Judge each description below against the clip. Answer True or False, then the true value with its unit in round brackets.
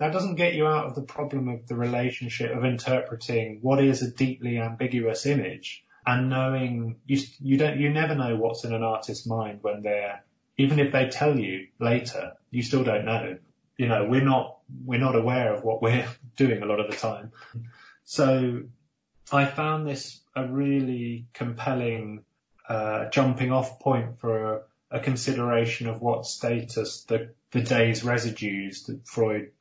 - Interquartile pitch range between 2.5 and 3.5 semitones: True (2.9 semitones)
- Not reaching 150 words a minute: False (170 wpm)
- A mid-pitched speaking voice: False (125 Hz)